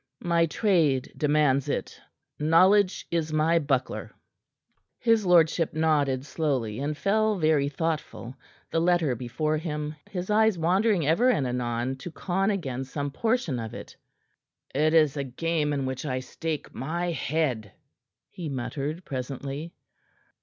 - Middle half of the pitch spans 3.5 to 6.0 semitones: Yes, average, 4.1 semitones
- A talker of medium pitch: Yes, medium, 155 Hz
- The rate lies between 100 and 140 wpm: Yes, slow, 135 wpm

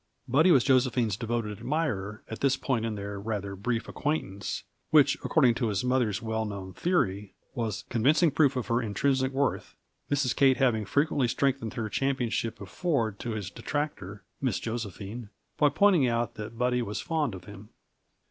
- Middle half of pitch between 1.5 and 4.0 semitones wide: No, average, 4.4 semitones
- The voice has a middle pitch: No, low, 115 Hz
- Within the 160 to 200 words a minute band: Yes, average, 165 wpm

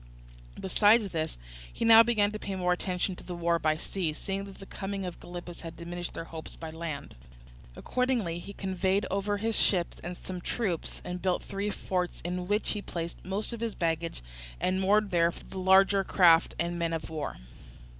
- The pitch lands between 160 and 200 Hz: Yes, medium, 185 Hz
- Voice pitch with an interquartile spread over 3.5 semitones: No, average, 2.9 semitones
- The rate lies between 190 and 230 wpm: Yes, average, 200 wpm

